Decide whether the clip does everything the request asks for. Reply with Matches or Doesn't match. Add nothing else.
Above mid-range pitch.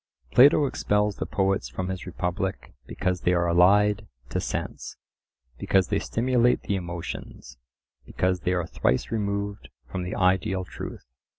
Doesn't match